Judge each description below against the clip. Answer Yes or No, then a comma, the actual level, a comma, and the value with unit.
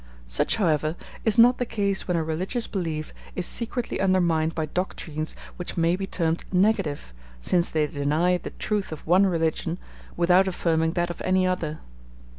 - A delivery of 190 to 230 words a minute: No, average, 165 wpm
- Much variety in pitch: No, average, 3.1 semitones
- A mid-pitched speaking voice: Yes, medium, 175 Hz